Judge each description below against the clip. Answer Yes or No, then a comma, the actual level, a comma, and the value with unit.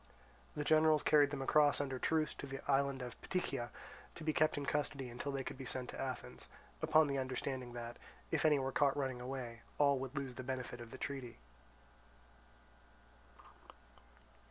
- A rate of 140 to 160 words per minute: No, average, 175 wpm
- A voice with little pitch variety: Yes, narrow, 2.2 semitones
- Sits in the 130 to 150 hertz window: Yes, low, 135 Hz